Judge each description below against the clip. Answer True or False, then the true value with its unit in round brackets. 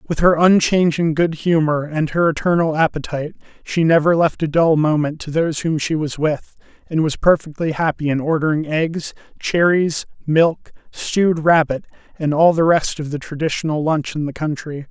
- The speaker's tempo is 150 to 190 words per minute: True (175 wpm)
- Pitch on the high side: False (160 Hz)